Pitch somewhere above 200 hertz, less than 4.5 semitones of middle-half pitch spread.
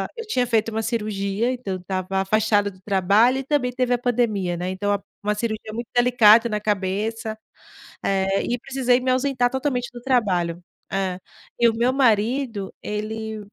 Yes: high, 220 Hz; average, 3.7 semitones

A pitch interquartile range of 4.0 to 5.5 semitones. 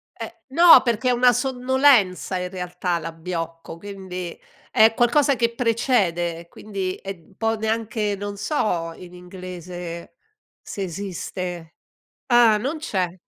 Yes: average, 4.7 semitones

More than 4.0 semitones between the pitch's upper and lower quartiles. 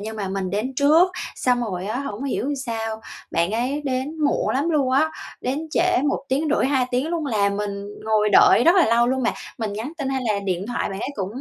Yes: average, 5.1 semitones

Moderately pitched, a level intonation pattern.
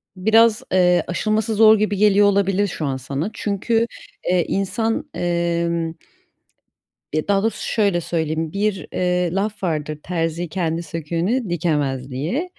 No: medium, 180 Hz; average, 4.0 semitones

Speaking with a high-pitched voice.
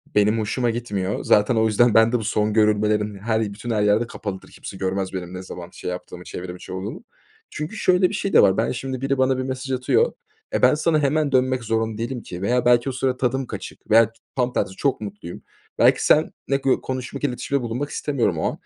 No: low, 115 Hz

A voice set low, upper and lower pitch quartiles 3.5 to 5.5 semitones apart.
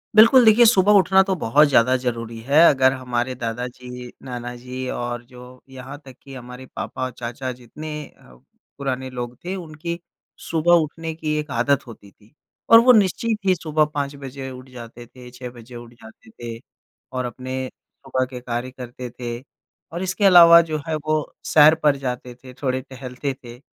Yes: low, 130 Hz; average, 4.0 semitones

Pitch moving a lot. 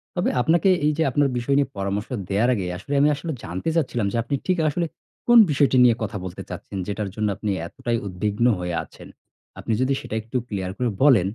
Yes: wide, 6.0 semitones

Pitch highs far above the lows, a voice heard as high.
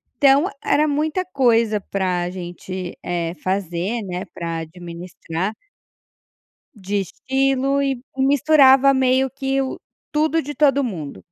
Yes: wide, 7.3 semitones; high, 240 Hz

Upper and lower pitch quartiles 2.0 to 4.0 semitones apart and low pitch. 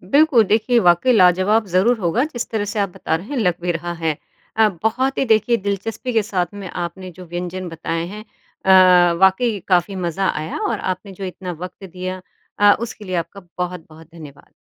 No: average, 3.5 semitones; medium, 185 Hz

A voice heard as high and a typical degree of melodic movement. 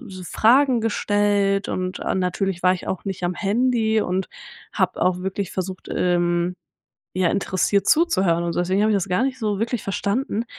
Yes: high, 195 Hz; average, 3.0 semitones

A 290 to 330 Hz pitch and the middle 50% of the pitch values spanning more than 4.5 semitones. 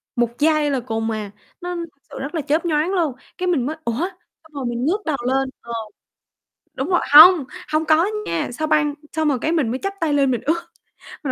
No: very high, 300 Hz; average, 4.0 semitones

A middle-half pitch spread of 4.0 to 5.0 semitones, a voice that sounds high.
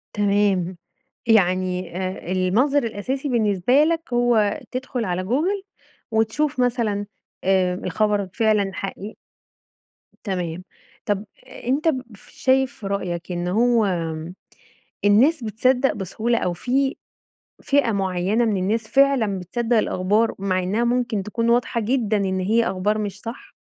Yes: average, 4.3 semitones; high, 215 Hz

